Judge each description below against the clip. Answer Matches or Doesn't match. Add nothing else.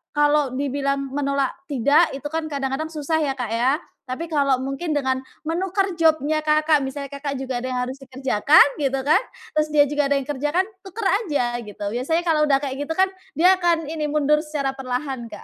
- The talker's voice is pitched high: Matches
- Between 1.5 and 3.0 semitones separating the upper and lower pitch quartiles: Matches